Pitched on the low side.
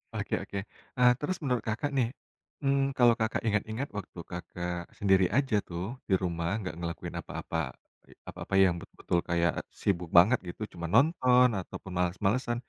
Yes: low, 105 Hz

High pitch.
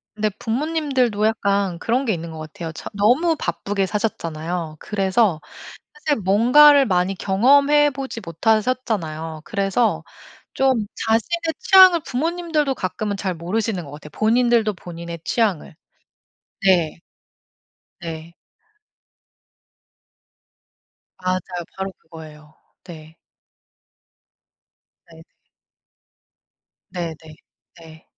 Yes: high, 205 Hz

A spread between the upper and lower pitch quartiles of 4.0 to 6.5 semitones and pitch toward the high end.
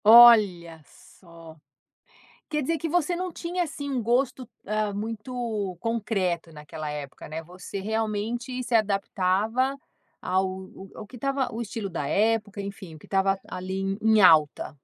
Yes: average, 4.4 semitones; high, 210 Hz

